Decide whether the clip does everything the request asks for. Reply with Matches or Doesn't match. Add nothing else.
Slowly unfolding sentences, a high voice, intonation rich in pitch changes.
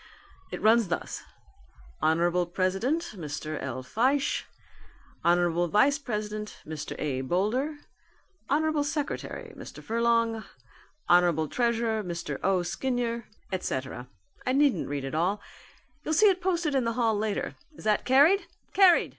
Matches